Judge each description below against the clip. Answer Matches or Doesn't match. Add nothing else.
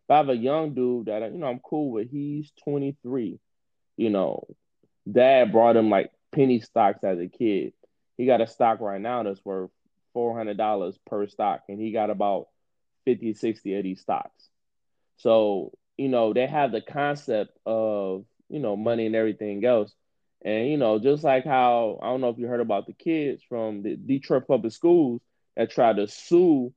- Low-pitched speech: Matches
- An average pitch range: Matches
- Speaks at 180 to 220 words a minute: Matches